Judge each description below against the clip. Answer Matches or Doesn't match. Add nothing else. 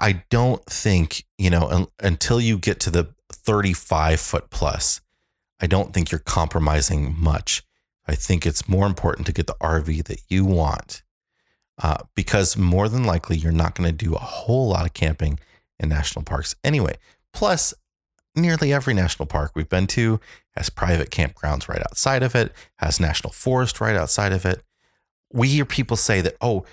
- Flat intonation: Doesn't match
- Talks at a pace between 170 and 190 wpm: Matches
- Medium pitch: Doesn't match